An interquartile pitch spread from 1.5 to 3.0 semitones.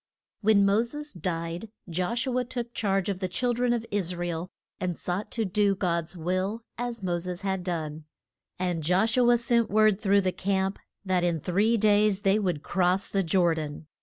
No: average, 3.5 semitones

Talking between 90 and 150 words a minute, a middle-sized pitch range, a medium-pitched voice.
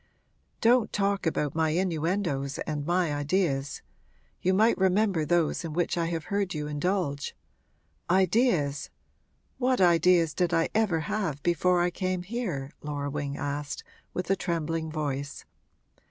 Yes: average, 140 wpm; average, 4.2 semitones; medium, 170 Hz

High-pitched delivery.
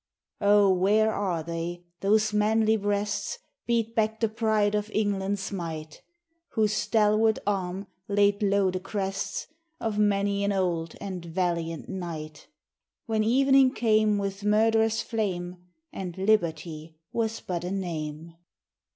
Yes: high, 200 Hz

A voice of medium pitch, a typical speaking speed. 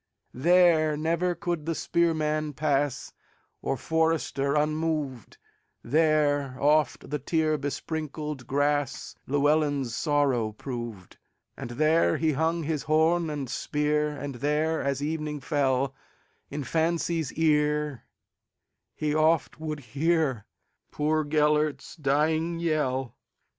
No: medium, 150 Hz; slow, 90 wpm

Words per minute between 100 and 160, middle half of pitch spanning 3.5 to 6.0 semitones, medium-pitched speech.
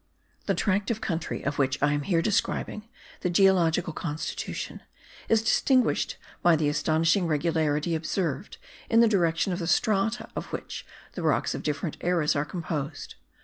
Yes: average, 155 wpm; average, 4.3 semitones; medium, 170 Hz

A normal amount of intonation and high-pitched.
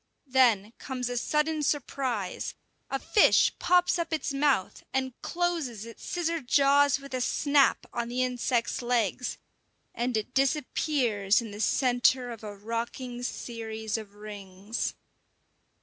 Yes: average, 3.9 semitones; very high, 250 Hz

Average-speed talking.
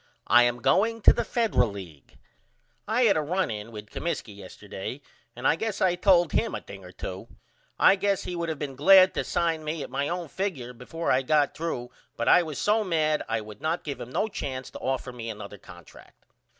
No: fast, 215 wpm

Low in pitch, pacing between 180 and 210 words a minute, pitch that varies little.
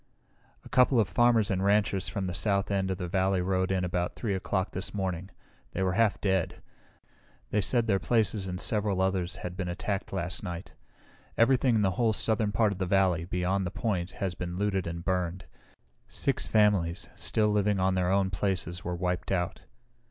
Yes: very low, 95 Hz; average, 190 wpm; narrow, 2.3 semitones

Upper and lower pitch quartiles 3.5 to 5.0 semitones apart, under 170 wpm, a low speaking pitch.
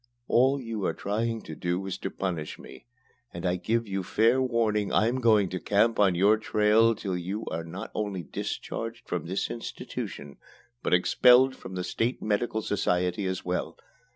No: average, 4.0 semitones; average, 175 wpm; low, 105 Hz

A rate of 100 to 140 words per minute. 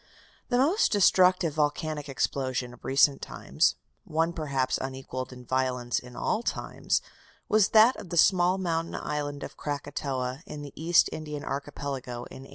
No: average, 155 wpm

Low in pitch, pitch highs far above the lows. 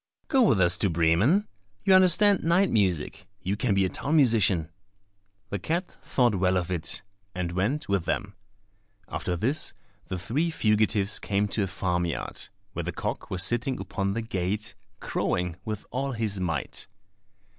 Yes: low, 100 Hz; wide, 6.0 semitones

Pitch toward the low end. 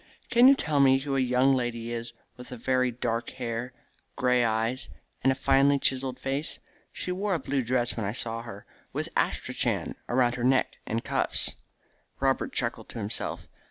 Yes: low, 125 Hz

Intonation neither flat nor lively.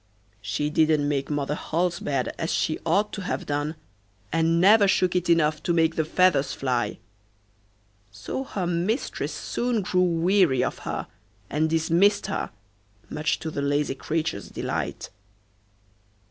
Yes: average, 3.6 semitones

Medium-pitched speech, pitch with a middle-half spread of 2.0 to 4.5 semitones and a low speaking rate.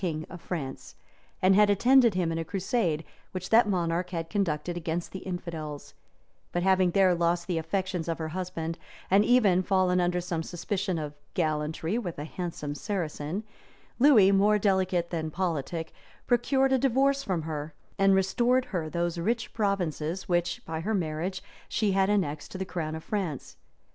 No: medium, 180 Hz; average, 3.3 semitones; average, 165 wpm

